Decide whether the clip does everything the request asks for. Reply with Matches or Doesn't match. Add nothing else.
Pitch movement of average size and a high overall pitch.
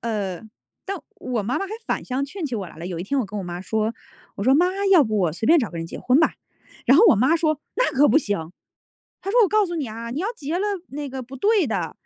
Doesn't match